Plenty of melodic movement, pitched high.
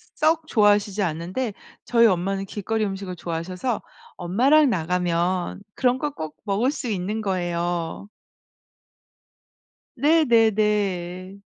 No: average, 4.5 semitones; high, 200 Hz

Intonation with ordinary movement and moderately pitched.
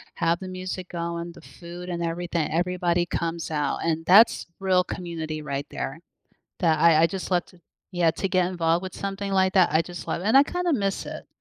No: narrow, 2.0 semitones; medium, 175 Hz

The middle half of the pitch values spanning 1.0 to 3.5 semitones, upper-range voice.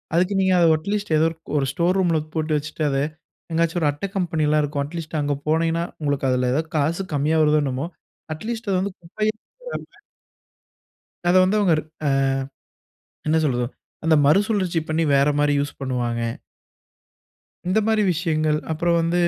No: average, 3.2 semitones; medium, 160 Hz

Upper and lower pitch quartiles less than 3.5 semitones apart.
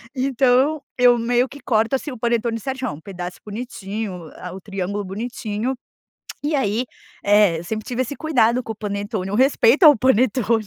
No: average, 4.0 semitones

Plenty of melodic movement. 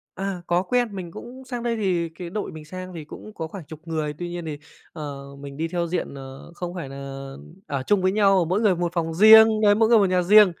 No: average, 4.2 semitones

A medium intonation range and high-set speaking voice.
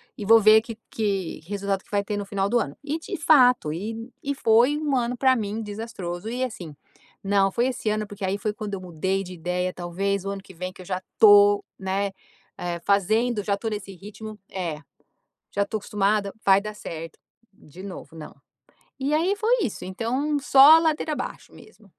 Yes: average, 3.4 semitones; high, 205 Hz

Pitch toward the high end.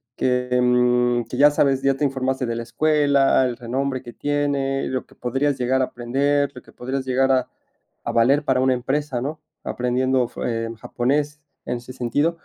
No: low, 130 Hz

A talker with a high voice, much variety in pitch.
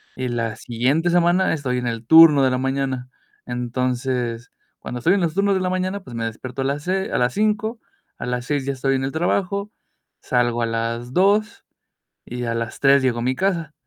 No: low, 135 Hz; wide, 6.2 semitones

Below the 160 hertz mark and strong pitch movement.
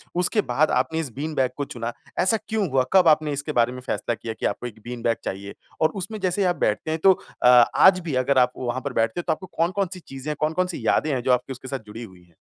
Yes: medium, 140 Hz; wide, 6.0 semitones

